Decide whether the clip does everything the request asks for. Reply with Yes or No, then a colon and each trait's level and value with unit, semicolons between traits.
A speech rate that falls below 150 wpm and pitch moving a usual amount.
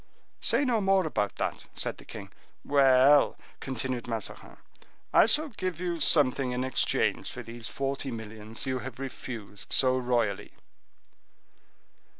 Yes: slow, 135 wpm; average, 3.9 semitones